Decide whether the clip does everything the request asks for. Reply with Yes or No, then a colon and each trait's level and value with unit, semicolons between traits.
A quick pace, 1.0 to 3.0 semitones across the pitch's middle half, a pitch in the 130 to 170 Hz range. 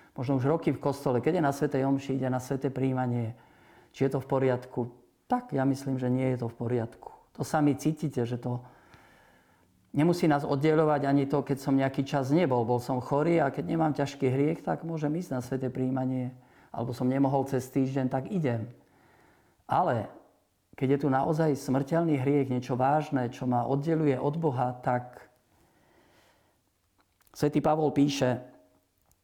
Yes: fast, 170 wpm; average, 2.7 semitones; low, 135 Hz